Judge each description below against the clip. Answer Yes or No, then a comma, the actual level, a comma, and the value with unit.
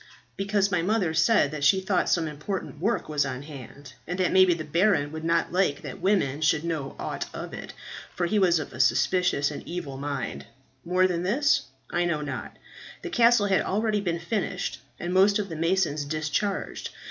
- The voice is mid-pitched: Yes, medium, 170 Hz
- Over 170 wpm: Yes, average, 190 wpm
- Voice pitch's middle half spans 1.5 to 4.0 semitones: No, average, 4.4 semitones